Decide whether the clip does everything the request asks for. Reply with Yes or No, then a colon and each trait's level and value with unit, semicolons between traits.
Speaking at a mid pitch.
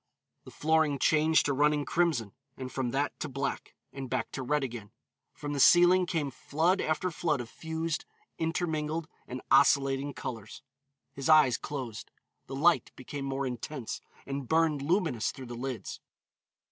Yes: medium, 145 Hz